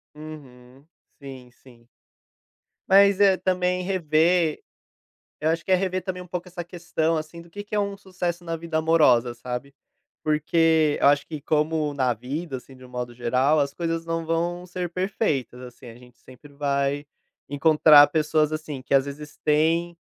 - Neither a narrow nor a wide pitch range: Yes, average, 3.8 semitones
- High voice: No, medium, 155 Hz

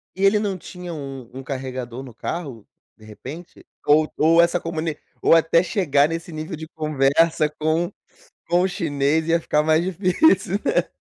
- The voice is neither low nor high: Yes, medium, 160 Hz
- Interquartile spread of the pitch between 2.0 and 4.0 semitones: Yes, average, 3.5 semitones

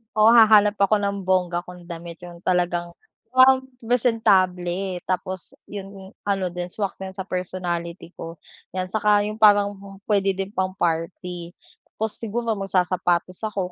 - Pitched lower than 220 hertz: Yes, high, 190 Hz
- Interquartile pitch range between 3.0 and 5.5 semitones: No, narrow, 2.6 semitones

